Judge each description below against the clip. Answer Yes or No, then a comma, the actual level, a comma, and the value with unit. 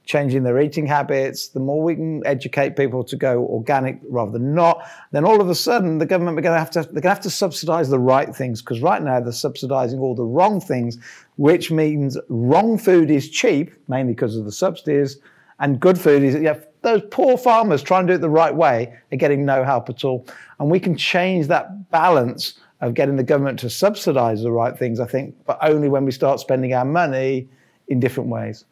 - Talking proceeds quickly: Yes, fast, 220 wpm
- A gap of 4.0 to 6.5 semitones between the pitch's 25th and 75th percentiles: Yes, average, 4.4 semitones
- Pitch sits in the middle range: Yes, medium, 145 Hz